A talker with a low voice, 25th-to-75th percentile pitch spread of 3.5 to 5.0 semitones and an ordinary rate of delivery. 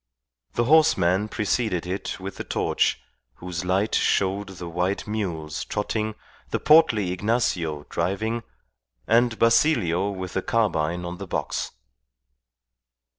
No: low, 100 Hz; average, 3.8 semitones; slow, 120 wpm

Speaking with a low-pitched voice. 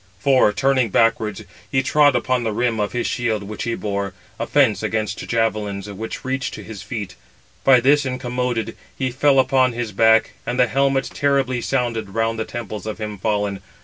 Yes: low, 115 Hz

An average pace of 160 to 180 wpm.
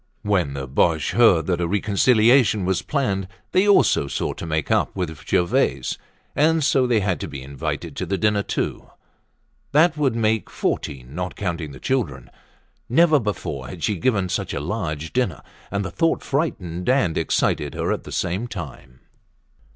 Yes: average, 170 wpm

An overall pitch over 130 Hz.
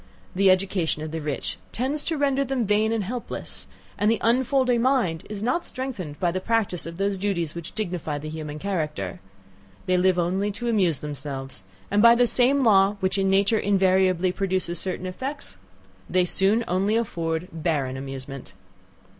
Yes: high, 190 Hz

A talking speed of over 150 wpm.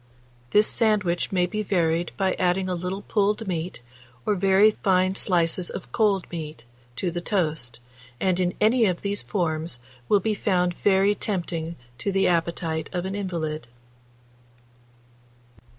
No: average, 145 wpm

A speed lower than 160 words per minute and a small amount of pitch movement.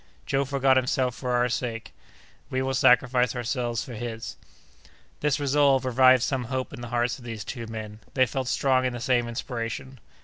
No: average, 180 wpm; narrow, 1.8 semitones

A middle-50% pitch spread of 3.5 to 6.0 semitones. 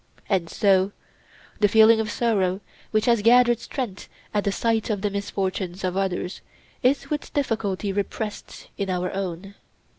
No: average, 2.8 semitones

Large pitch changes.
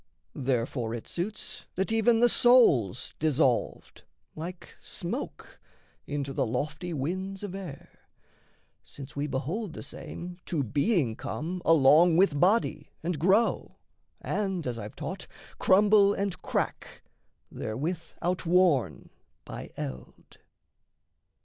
Yes: wide, 6.0 semitones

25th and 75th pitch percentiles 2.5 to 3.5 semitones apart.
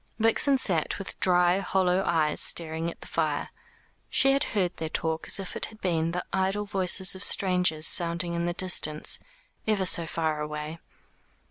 Yes: average, 2.9 semitones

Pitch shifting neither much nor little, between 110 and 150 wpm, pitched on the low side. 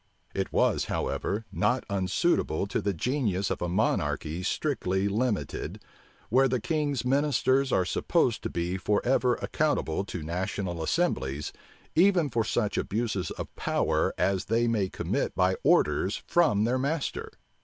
No: wide, 6.0 semitones; average, 140 wpm; low, 105 Hz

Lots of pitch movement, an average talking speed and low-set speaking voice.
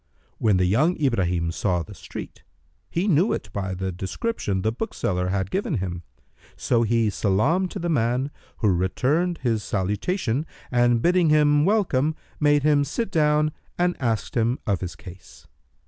Yes: wide, 8.3 semitones; average, 160 wpm; low, 120 Hz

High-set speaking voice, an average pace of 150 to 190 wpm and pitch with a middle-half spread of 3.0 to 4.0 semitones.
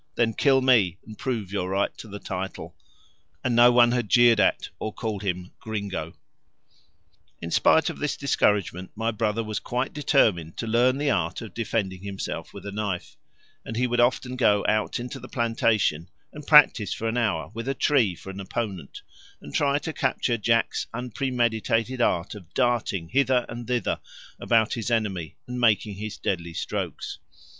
No: low, 115 Hz; average, 175 wpm; average, 3.7 semitones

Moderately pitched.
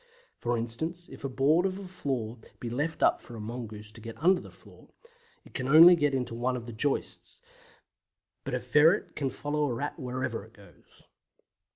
No: low, 130 Hz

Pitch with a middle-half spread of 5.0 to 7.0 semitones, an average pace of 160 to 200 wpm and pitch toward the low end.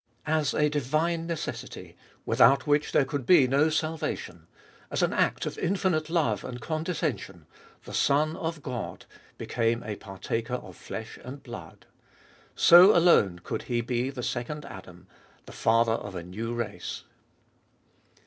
No: wide, 5.5 semitones; average, 150 wpm; low, 130 Hz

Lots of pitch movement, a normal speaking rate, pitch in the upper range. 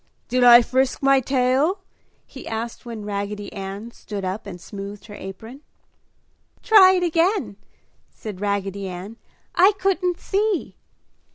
No: wide, 8.4 semitones; slow, 130 wpm; high, 230 Hz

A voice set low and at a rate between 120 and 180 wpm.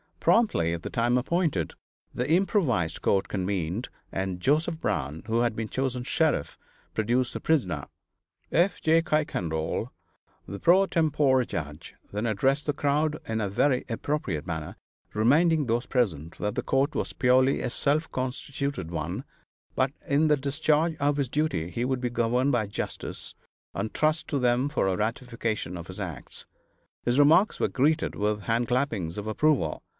Yes: low, 125 Hz; average, 160 wpm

